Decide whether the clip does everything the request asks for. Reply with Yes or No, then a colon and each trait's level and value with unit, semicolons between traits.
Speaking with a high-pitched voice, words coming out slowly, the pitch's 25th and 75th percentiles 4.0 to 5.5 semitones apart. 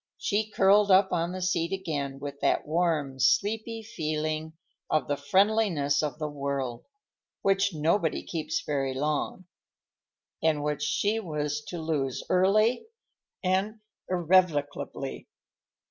No: medium, 160 Hz; slow, 115 wpm; average, 4.9 semitones